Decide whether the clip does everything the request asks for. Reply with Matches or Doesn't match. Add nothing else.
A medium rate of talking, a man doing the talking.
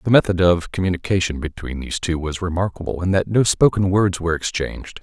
Matches